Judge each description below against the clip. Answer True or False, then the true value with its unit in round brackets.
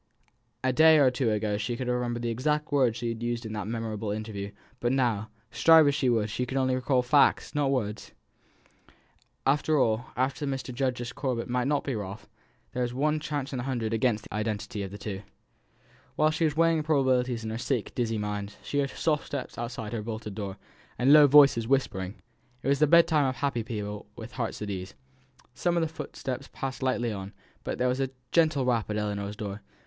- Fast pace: True (210 wpm)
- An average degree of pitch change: True (4.1 semitones)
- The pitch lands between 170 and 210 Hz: False (125 Hz)